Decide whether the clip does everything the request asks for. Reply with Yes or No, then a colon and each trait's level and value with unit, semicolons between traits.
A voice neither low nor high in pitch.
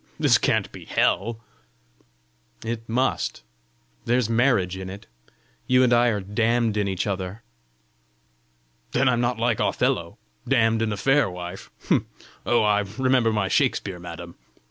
No: low, 115 Hz